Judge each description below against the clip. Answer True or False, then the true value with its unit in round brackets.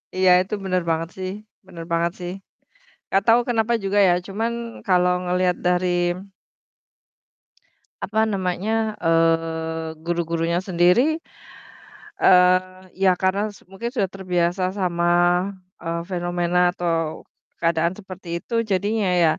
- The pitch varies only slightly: True (2.1 semitones)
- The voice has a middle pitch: True (180 Hz)